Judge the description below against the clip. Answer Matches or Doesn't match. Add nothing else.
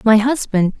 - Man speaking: Doesn't match